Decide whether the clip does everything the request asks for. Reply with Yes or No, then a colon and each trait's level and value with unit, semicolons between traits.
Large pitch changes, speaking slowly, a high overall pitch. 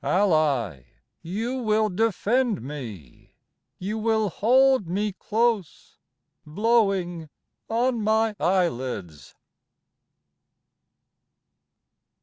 Yes: wide, 6.1 semitones; slow, 70 wpm; high, 205 Hz